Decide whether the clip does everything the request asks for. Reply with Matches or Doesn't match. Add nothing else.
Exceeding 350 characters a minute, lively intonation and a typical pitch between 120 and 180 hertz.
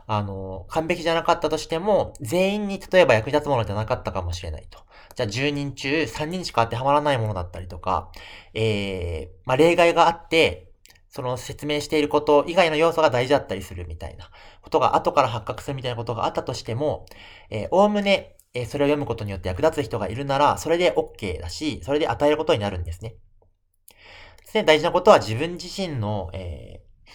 Matches